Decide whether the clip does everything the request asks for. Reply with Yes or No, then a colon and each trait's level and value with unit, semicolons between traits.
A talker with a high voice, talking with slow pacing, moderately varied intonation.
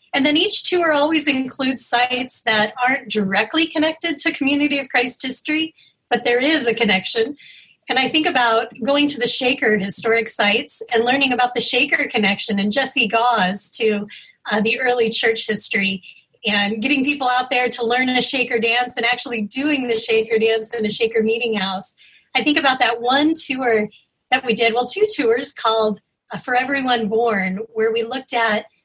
No: high, 240 Hz; average, 185 wpm; average, 3.0 semitones